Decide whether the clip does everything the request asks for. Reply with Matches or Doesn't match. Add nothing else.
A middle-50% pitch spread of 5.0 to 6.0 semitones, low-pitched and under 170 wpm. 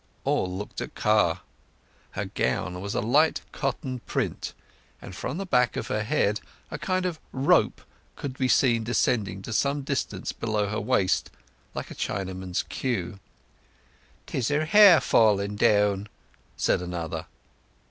Matches